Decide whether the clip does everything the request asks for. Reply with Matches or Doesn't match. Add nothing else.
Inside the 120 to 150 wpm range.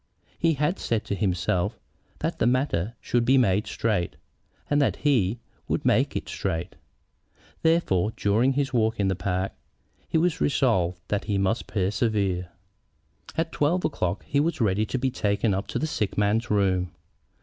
Doesn't match